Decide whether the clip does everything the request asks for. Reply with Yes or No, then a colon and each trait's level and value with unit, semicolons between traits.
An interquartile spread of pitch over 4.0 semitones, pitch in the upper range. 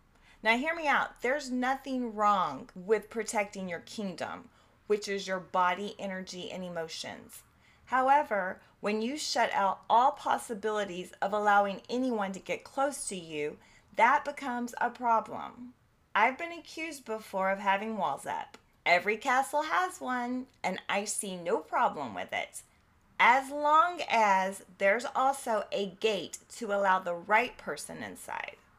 Yes: average, 4.8 semitones; high, 215 Hz